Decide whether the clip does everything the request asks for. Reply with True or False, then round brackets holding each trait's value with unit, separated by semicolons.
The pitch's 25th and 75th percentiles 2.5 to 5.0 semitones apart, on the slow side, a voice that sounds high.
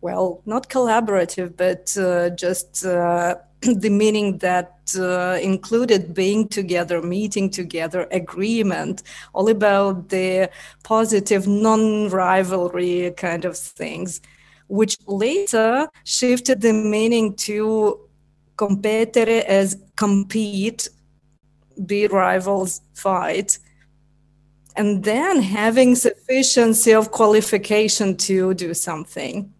True (3.3 semitones; 95 wpm; 195 Hz)